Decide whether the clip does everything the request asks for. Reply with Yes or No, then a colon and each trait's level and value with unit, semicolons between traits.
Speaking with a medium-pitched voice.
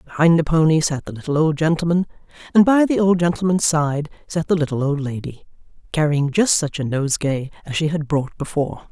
Yes: medium, 155 Hz